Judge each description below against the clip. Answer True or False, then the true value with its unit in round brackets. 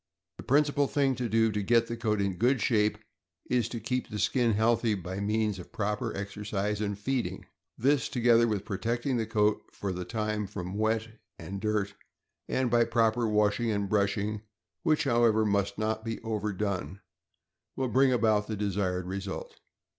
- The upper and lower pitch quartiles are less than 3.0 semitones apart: True (2.5 semitones)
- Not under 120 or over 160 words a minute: False (170 wpm)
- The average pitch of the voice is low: True (110 Hz)